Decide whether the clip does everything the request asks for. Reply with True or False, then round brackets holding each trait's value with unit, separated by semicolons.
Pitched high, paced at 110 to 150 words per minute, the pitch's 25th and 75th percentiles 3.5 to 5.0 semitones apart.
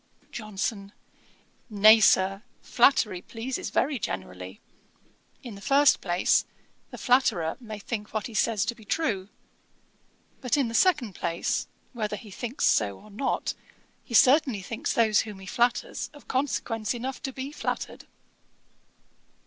True (220 Hz; 140 wpm; 4.2 semitones)